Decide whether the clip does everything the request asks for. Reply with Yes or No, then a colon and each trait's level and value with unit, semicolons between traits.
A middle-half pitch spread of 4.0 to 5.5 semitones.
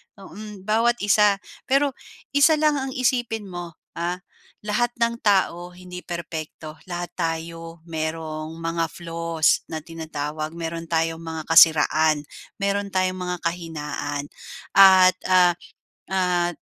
No: average, 3.5 semitones